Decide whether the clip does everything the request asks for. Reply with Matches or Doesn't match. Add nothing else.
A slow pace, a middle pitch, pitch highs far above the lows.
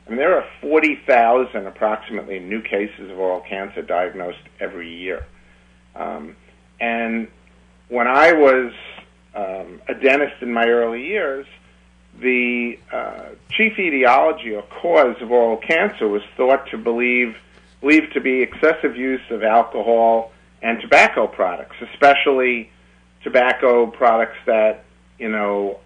Doesn't match